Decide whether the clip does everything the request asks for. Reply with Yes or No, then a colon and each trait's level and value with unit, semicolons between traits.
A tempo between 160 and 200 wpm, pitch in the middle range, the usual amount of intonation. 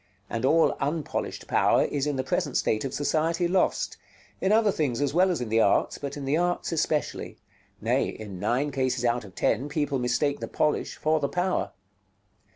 Yes: average, 190 wpm; medium, 145 Hz; average, 4.6 semitones